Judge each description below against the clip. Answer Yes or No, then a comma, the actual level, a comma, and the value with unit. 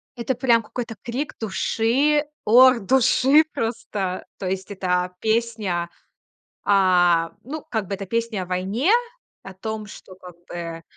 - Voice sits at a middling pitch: No, high, 215 Hz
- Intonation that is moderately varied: Yes, average, 4.3 semitones